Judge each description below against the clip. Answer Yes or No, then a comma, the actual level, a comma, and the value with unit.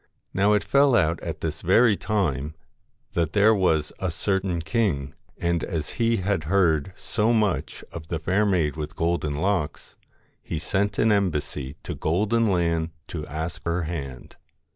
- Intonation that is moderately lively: Yes, average, 4.5 semitones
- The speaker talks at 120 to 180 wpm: Yes, average, 160 wpm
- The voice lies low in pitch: Yes, very low, 85 Hz